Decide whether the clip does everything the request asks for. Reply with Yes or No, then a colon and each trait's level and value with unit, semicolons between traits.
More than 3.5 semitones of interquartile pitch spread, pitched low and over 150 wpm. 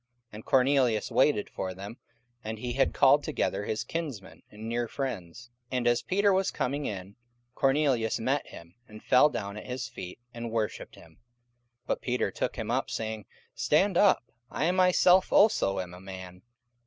Yes: average, 5.2 semitones; low, 120 Hz; average, 175 wpm